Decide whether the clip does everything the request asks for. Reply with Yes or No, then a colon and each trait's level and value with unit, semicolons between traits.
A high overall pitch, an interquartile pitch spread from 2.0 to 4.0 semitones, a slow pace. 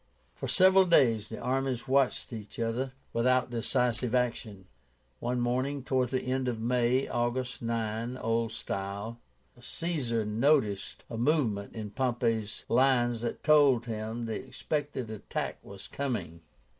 No: low, 120 Hz; narrow, 2.6 semitones; slow, 130 wpm